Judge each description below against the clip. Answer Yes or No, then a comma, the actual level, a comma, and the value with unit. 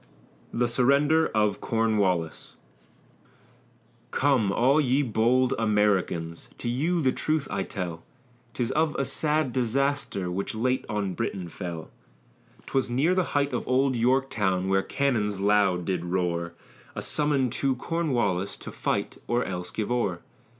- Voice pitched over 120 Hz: No, low, 115 Hz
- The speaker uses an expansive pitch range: Yes, wide, 5.9 semitones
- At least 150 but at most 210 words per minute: No, average, 140 wpm